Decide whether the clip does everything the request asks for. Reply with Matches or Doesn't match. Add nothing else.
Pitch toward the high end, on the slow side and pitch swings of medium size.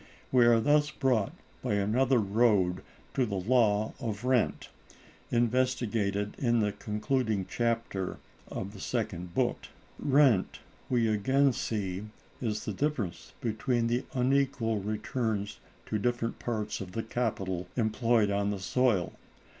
Doesn't match